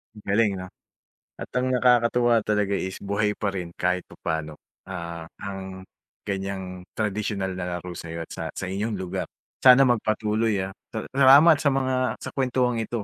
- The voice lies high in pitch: No, low, 105 Hz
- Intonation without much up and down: No, average, 4.2 semitones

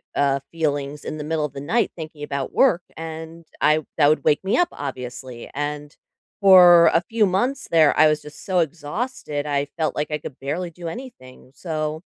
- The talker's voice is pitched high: No, medium, 155 Hz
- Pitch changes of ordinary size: Yes, average, 3.0 semitones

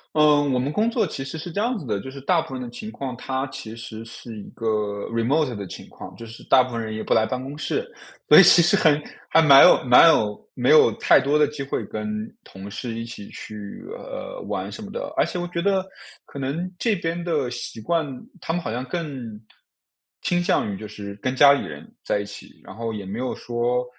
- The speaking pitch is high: No, low, 135 Hz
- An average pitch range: No, wide, 6.2 semitones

